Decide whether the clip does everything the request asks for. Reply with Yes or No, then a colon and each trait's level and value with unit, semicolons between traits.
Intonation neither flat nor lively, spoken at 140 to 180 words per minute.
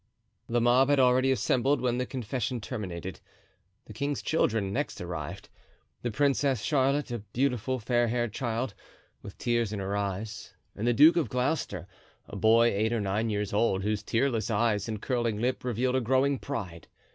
Yes: average, 3.7 semitones; average, 170 wpm